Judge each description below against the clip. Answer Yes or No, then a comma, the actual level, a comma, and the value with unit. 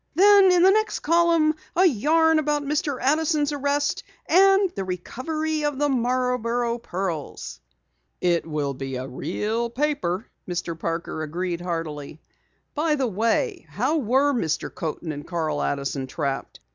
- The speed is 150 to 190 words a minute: No, average, 140 wpm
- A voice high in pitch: Yes, very high, 250 Hz